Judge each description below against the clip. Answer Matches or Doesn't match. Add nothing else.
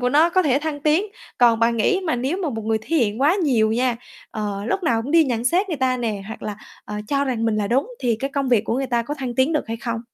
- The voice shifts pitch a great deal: Doesn't match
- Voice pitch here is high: Matches